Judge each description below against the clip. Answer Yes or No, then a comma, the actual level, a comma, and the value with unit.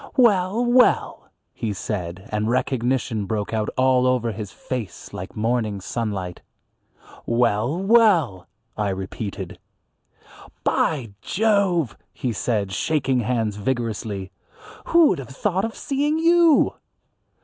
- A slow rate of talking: Yes, slow, 115 wpm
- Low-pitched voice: Yes, low, 120 Hz